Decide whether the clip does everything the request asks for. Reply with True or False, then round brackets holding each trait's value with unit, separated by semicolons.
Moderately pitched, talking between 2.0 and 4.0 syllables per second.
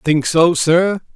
True (165 Hz; 3.1 syllables/s)